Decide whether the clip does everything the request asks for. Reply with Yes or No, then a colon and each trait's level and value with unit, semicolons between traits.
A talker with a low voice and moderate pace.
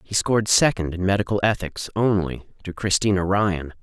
Yes: very low, 95 Hz; average, 155 wpm